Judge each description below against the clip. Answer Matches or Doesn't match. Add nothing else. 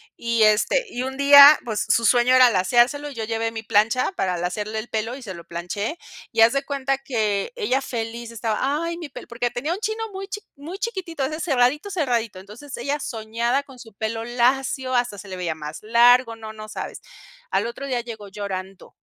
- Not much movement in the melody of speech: Doesn't match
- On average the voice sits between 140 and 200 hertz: Doesn't match